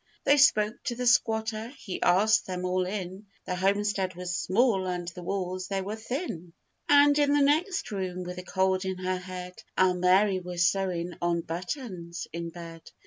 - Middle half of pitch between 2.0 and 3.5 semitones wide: Yes, average, 3.2 semitones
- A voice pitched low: No, medium, 185 Hz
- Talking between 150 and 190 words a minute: Yes, average, 180 wpm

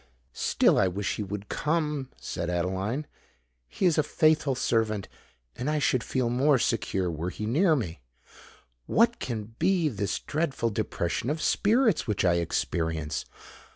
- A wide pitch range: Yes, wide, 8.2 semitones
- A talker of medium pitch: No, low, 115 Hz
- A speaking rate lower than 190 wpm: Yes, average, 145 wpm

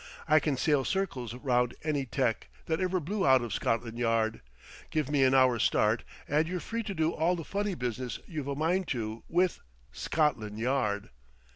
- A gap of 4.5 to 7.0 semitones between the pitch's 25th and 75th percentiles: Yes, average, 5.3 semitones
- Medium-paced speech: Yes, average, 180 wpm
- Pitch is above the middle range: No, low, 135 Hz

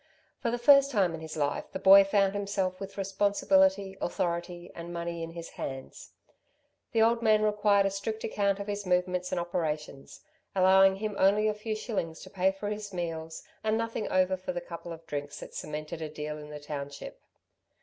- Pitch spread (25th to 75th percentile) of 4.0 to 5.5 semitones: No, average, 3.4 semitones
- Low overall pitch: No, high, 190 Hz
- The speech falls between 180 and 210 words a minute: Yes, average, 190 wpm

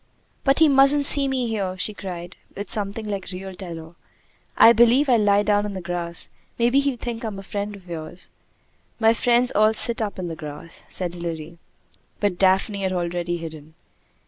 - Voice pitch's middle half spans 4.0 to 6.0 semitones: Yes, average, 4.8 semitones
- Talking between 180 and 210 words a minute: Yes, average, 190 wpm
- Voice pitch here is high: Yes, high, 200 Hz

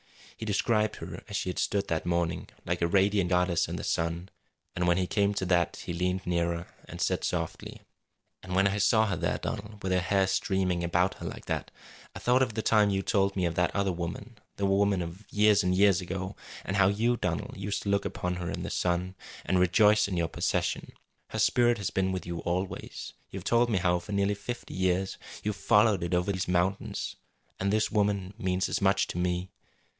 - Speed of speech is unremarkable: No, fast, 220 wpm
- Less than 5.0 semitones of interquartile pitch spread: Yes, narrow, 2.4 semitones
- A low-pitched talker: Yes, very low, 95 Hz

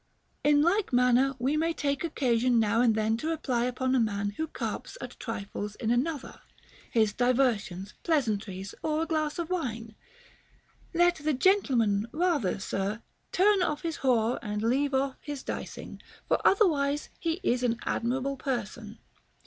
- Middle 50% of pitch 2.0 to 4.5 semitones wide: No, wide, 5.4 semitones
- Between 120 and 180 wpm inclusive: Yes, average, 160 wpm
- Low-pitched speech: No, very high, 255 Hz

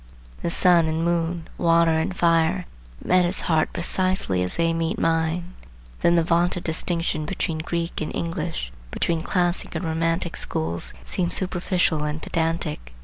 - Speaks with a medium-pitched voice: Yes, medium, 165 Hz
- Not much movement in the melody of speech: Yes, narrow, 1.5 semitones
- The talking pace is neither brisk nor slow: Yes, average, 145 wpm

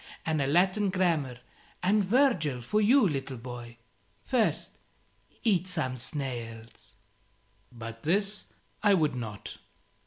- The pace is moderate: No, slow, 115 wpm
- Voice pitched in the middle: Yes, medium, 155 Hz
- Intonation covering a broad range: Yes, wide, 8.3 semitones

